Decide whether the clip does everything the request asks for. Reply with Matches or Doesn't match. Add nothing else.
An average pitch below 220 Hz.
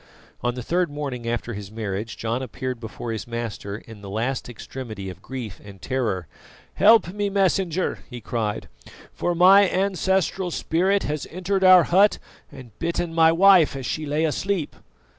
Matches